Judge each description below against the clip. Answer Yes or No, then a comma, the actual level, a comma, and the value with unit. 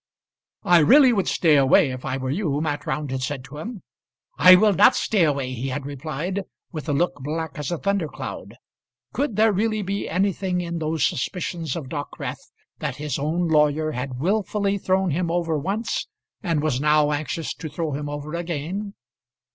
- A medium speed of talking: Yes, average, 180 wpm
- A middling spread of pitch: Yes, average, 4.4 semitones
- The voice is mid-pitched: Yes, medium, 160 Hz